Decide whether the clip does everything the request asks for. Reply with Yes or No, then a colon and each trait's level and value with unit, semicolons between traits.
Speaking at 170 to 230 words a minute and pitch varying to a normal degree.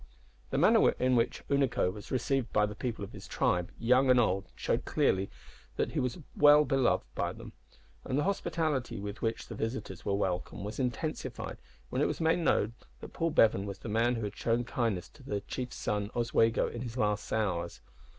Yes: average, 200 wpm; average, 4.1 semitones